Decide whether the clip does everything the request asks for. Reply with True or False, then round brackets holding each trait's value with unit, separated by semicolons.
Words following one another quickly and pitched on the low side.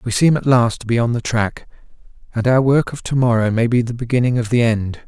True (260 wpm; 120 Hz)